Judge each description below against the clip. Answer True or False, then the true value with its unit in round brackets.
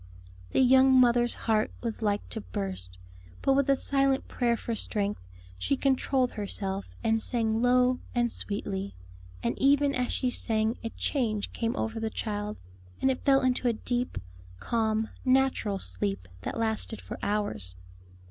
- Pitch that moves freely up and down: False (3.7 semitones)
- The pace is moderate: True (155 wpm)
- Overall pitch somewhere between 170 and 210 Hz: False (225 Hz)